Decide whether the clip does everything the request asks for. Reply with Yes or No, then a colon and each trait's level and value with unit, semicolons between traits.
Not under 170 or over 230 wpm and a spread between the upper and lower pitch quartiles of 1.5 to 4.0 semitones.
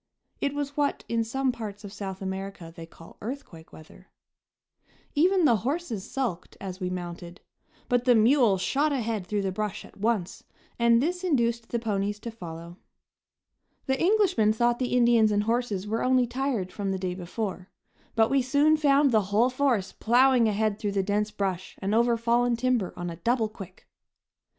No: average, 175 wpm; average, 4.5 semitones